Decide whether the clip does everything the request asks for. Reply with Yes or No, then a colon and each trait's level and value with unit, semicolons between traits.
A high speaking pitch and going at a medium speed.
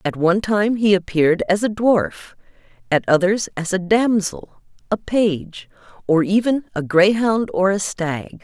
Yes: high, 195 Hz; average, 155 wpm